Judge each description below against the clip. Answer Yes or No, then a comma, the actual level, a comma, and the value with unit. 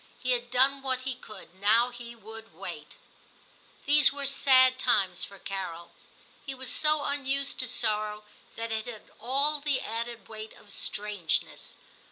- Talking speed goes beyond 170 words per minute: No, average, 155 wpm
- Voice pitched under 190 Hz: No, high, 240 Hz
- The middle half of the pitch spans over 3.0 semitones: Yes, average, 3.8 semitones